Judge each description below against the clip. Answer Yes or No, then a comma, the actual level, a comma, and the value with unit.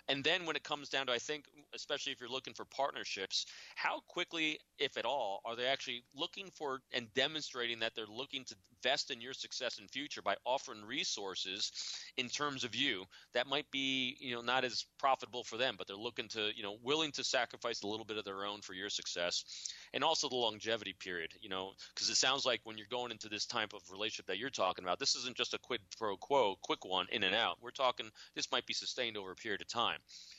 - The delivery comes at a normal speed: No, fast, 235 wpm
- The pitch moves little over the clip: No, average, 4.1 semitones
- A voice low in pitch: Yes, low, 125 Hz